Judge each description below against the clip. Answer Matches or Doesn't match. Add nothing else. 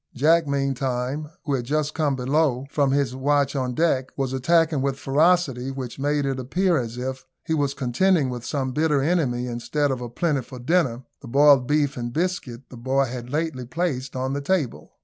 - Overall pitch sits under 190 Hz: Matches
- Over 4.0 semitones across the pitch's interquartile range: Doesn't match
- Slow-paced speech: Doesn't match